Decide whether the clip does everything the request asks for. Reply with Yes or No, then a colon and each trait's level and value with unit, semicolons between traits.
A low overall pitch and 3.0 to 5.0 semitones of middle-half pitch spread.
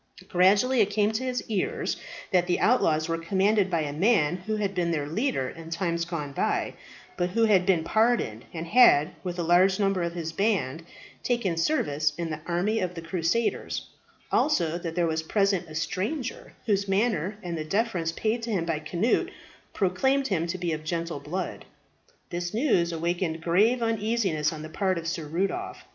No: medium, 180 Hz; average, 4.2 semitones